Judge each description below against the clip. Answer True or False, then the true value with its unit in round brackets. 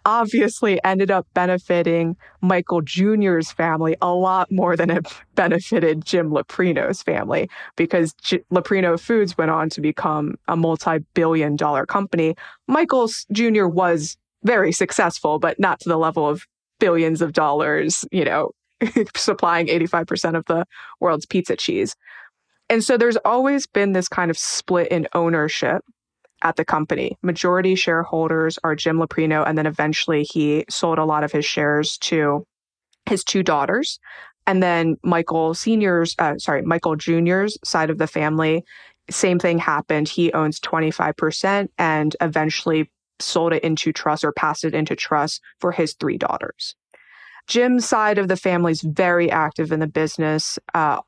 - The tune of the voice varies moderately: True (3.0 semitones)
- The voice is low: False (170 Hz)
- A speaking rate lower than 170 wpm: True (155 wpm)